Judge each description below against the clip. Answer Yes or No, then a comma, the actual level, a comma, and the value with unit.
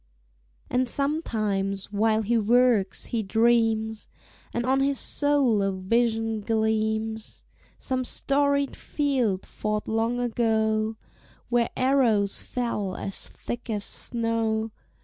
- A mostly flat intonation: Yes, narrow, 2.2 semitones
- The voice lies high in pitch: Yes, high, 225 Hz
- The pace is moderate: No, slow, 110 wpm